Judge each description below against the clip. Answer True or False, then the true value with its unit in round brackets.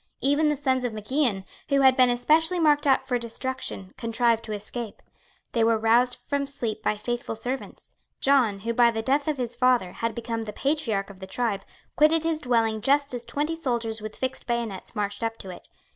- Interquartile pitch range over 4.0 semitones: False (3.6 semitones)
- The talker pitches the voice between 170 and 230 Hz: False (240 Hz)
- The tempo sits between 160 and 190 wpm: False (205 wpm)